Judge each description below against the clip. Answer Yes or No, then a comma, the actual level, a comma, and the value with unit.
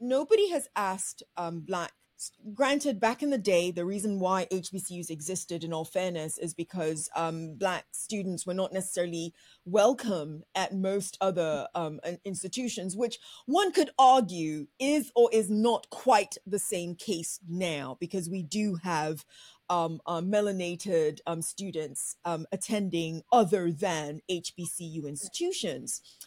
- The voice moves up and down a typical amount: Yes, average, 3.9 semitones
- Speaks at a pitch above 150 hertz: Yes, medium, 185 Hz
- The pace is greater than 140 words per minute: No, slow, 135 wpm